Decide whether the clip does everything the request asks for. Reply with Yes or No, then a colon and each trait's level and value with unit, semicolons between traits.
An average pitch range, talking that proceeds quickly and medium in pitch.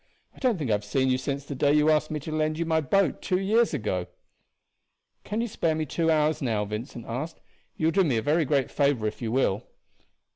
Yes: average, 4.2 semitones; fast, 240 wpm; medium, 150 Hz